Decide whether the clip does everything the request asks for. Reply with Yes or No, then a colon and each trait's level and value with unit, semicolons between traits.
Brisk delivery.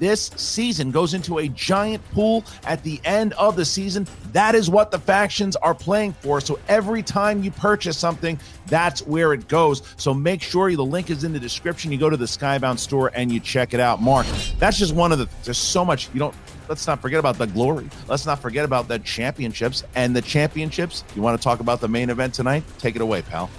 Yes: fast, 230 wpm